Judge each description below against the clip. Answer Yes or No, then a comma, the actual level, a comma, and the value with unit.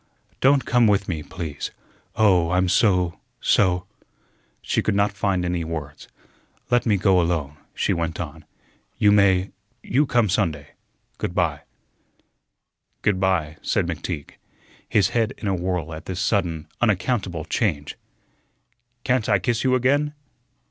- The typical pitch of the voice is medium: No, very low, 95 Hz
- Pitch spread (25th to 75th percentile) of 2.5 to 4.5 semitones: Yes, average, 4.0 semitones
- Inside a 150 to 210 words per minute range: No, average, 140 wpm